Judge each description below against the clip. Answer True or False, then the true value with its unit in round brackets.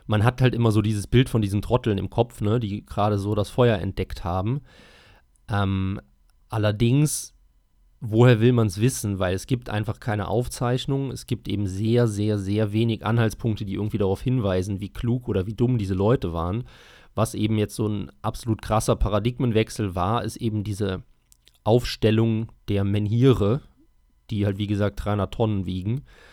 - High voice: False (105 Hz)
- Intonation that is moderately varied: True (3.1 semitones)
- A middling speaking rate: True (170 wpm)